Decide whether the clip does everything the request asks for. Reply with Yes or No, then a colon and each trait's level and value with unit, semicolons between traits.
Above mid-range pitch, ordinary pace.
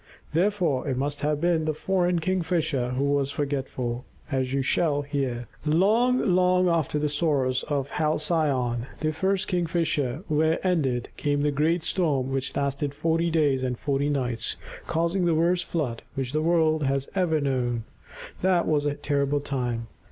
No: medium, 150 Hz; average, 160 wpm